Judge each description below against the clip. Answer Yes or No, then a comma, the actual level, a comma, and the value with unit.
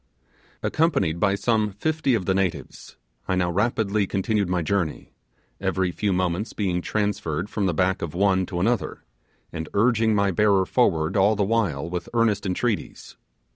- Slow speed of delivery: No, average, 160 wpm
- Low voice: Yes, low, 100 Hz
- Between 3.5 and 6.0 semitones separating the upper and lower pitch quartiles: No, average, 2.9 semitones